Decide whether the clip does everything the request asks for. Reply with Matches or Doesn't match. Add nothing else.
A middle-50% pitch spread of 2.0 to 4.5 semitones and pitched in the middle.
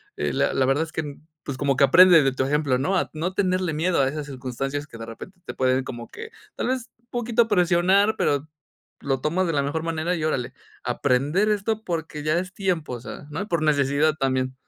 Doesn't match